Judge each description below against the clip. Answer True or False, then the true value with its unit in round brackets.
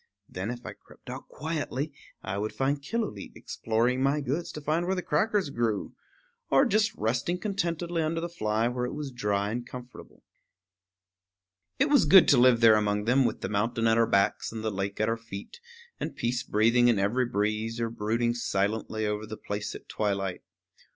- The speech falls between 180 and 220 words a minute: True (190 wpm)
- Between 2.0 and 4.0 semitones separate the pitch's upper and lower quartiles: False (5.3 semitones)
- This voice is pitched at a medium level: False (120 Hz)